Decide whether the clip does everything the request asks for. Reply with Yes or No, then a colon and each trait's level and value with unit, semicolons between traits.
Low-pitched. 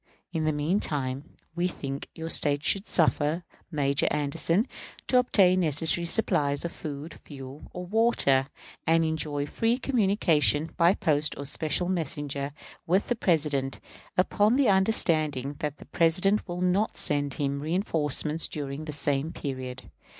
No: medium, 155 Hz